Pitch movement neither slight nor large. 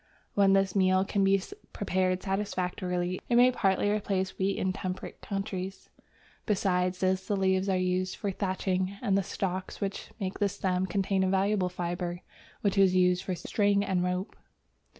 No: narrow, 1.3 semitones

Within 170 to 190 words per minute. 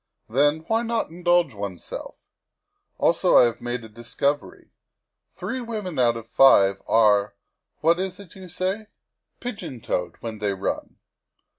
No: average, 140 wpm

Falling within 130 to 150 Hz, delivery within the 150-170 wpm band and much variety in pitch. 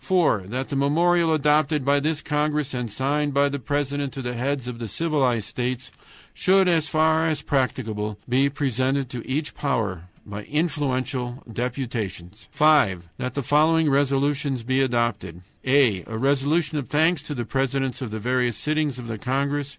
No: low, 135 Hz; average, 165 wpm; average, 3.4 semitones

